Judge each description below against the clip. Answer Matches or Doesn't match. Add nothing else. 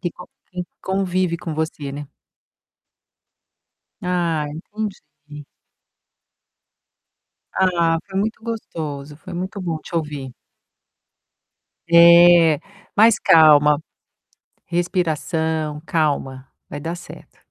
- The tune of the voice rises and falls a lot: Doesn't match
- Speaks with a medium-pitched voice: Matches